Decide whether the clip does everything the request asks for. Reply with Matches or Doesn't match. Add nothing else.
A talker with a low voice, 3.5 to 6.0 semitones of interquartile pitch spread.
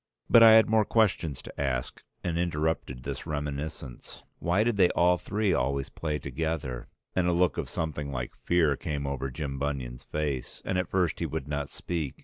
Matches